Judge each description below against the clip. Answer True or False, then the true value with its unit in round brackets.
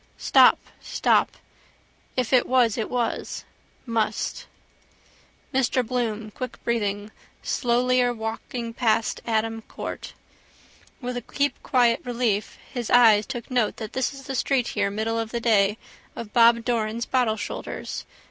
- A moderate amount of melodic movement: False (2.1 semitones)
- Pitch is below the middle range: False (235 Hz)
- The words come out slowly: True (130 wpm)